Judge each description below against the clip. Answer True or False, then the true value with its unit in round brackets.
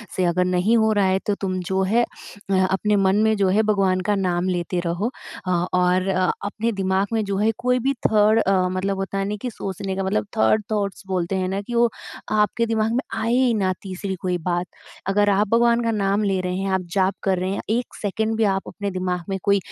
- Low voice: False (195 Hz)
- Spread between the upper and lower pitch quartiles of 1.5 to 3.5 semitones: True (2.4 semitones)